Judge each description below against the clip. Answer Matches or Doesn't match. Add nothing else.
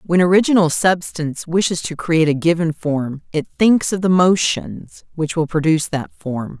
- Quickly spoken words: Doesn't match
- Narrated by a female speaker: Matches